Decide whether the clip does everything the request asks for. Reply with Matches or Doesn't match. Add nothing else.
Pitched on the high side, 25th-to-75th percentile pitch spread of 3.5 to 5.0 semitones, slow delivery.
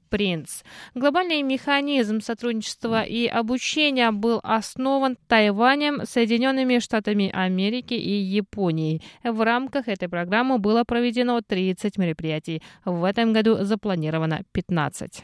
Matches